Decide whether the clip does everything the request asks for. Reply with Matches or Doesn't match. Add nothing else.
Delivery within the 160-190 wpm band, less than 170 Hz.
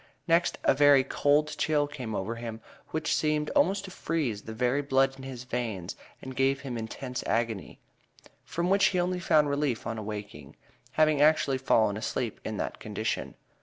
Matches